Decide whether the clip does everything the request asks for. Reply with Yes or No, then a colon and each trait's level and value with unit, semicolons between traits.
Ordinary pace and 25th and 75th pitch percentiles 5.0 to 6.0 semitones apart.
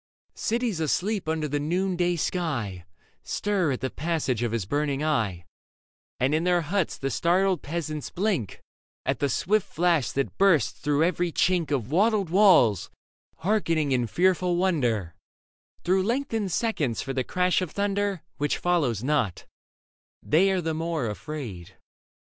Yes: average, 145 wpm; wide, 5.4 semitones